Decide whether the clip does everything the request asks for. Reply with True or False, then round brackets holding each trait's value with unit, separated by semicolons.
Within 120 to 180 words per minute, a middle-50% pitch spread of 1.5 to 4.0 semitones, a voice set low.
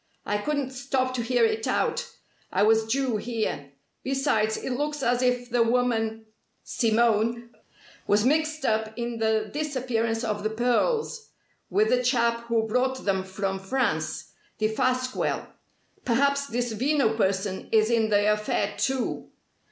False (140 wpm; 2.9 semitones; 235 Hz)